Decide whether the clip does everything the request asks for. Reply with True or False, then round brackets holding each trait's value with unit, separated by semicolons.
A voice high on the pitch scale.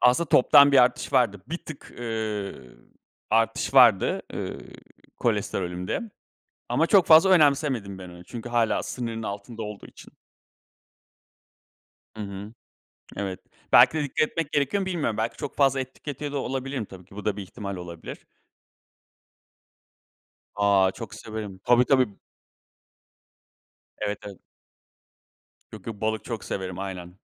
False (115 Hz)